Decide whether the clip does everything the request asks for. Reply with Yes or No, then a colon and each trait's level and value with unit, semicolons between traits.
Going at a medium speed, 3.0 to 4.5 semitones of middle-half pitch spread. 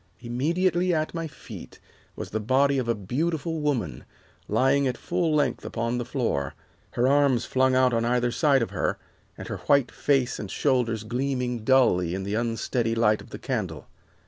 Yes: average, 175 wpm; average, 3.5 semitones